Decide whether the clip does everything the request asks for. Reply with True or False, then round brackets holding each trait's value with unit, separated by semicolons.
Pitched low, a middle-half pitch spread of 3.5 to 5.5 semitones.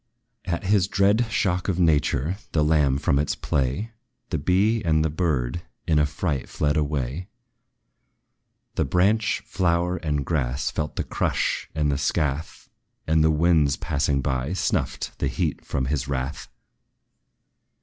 True (75 Hz; 4.1 semitones)